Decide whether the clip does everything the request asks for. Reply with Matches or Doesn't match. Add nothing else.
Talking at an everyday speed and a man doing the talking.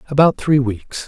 Matches